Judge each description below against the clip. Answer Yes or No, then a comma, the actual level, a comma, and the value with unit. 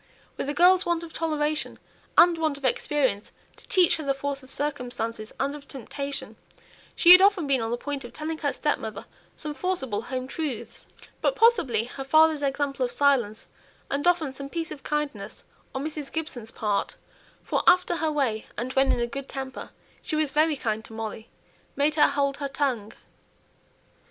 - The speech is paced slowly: No, average, 180 wpm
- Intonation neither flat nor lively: Yes, average, 3.3 semitones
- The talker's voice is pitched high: Yes, very high, 280 Hz